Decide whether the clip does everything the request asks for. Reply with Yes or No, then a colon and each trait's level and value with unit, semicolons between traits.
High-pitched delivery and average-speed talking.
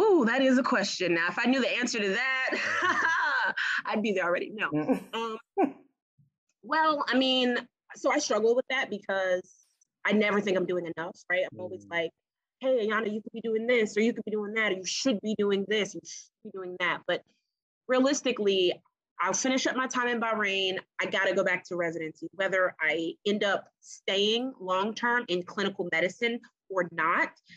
Yes: high, 210 Hz; average, 195 wpm